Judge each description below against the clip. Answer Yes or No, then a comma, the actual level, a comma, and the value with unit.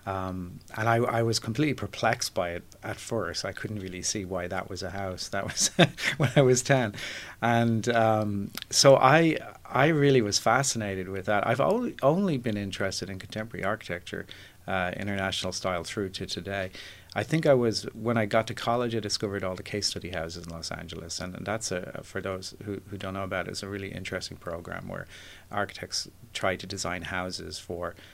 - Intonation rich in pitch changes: No, average, 3.4 semitones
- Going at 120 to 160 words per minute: No, average, 200 wpm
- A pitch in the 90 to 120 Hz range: Yes, low, 100 Hz